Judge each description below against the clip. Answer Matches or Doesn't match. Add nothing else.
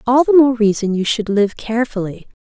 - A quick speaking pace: Doesn't match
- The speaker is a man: Doesn't match